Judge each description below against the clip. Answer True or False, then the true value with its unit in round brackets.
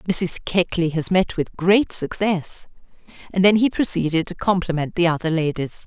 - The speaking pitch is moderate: True (175 Hz)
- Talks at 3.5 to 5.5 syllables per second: True (4.9 syllables/s)